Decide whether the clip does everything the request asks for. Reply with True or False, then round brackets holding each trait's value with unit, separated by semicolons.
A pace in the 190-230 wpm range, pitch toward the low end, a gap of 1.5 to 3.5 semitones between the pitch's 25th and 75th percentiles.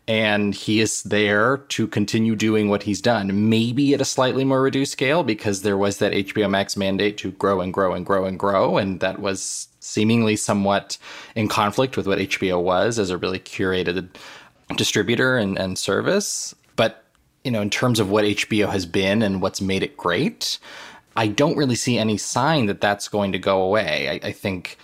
True (200 wpm; 105 Hz; 2.5 semitones)